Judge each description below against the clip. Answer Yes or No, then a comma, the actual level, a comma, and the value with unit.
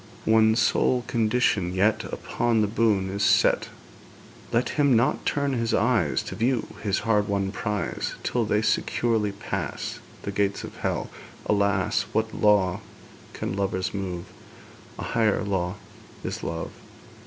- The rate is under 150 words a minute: Yes, average, 140 wpm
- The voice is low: Yes, low, 105 Hz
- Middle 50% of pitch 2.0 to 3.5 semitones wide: Yes, average, 2.7 semitones